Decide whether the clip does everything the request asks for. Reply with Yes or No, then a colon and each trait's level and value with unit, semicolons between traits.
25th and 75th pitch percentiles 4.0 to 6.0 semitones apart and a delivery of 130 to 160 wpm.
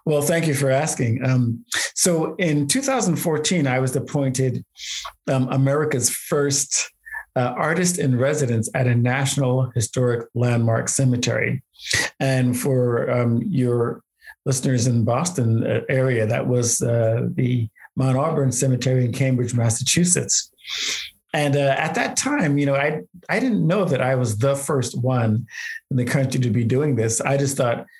No: average, 3.2 semitones; average, 150 wpm